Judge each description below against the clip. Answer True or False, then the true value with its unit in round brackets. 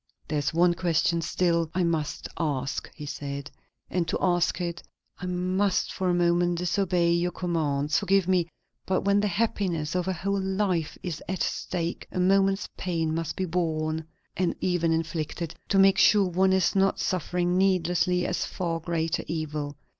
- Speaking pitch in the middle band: True (175 Hz)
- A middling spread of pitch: False (2.3 semitones)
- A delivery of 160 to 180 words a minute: True (170 wpm)